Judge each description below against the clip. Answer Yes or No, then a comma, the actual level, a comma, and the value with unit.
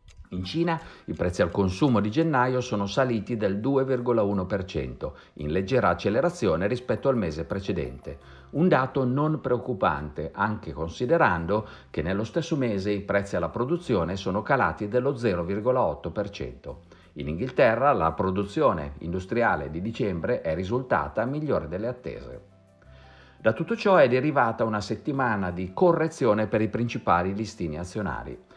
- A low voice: Yes, low, 105 Hz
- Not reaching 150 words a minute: Yes, average, 130 wpm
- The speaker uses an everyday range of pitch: No, wide, 6.1 semitones